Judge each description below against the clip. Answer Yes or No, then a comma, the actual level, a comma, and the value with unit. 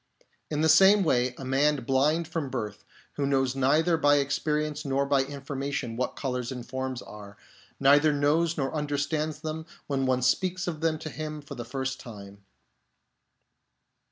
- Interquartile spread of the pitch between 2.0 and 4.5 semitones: Yes, average, 2.8 semitones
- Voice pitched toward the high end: No, medium, 140 Hz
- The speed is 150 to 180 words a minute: Yes, average, 165 wpm